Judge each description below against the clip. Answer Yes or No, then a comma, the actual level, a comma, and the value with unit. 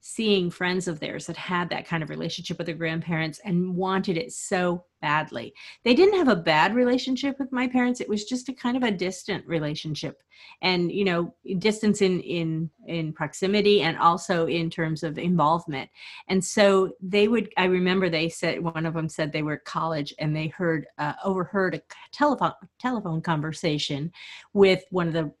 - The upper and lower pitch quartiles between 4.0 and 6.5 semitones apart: No, average, 3.4 semitones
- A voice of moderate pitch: Yes, medium, 175 Hz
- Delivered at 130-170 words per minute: No, average, 185 wpm